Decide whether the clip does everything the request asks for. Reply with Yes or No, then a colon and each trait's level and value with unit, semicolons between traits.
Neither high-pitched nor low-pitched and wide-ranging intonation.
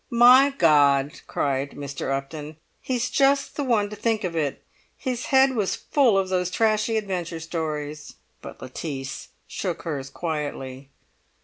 Yes: medium, 170 Hz; wide, 7.7 semitones